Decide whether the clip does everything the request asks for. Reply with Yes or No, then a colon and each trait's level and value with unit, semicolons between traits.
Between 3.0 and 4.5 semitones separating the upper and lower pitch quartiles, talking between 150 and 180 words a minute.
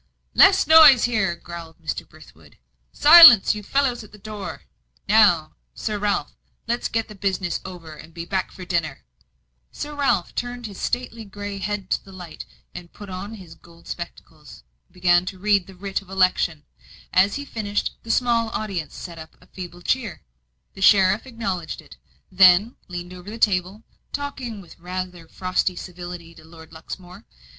Yes: average, 3.7 semitones; average, 165 wpm